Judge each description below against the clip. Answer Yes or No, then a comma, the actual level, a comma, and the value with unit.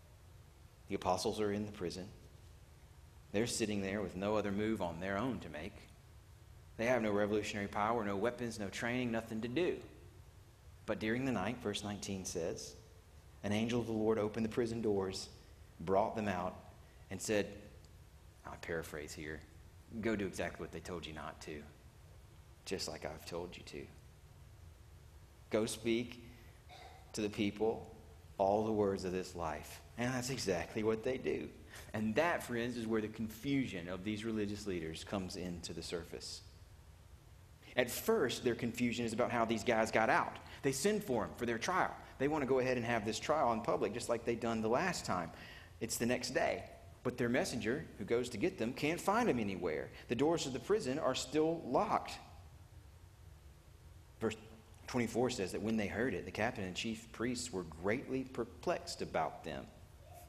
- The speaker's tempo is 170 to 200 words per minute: Yes, average, 180 wpm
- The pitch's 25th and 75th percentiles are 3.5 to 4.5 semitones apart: Yes, average, 4.2 semitones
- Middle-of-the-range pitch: No, low, 105 Hz